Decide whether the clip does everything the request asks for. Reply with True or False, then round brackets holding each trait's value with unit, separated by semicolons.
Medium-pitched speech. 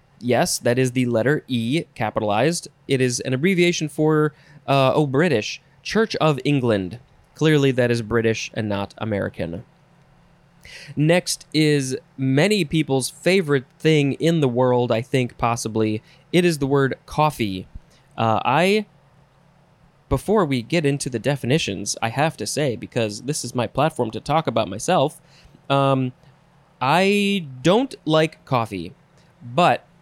True (145 Hz)